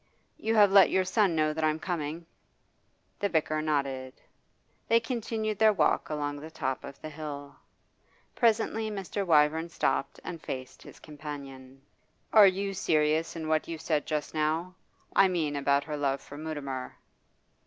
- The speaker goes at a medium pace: Yes, average, 160 wpm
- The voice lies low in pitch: No, medium, 155 Hz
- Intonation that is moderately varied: Yes, average, 4.6 semitones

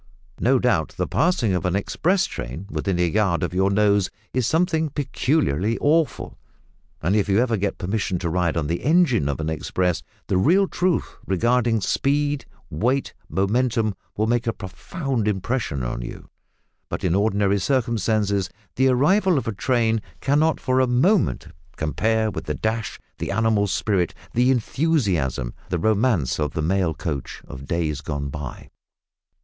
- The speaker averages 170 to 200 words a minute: No, average, 160 wpm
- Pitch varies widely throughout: Yes, wide, 6.4 semitones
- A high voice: No, low, 110 Hz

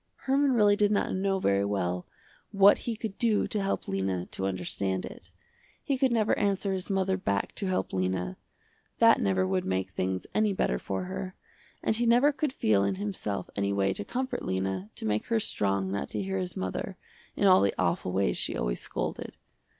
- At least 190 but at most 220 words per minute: Yes, average, 195 wpm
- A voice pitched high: No, low, 105 Hz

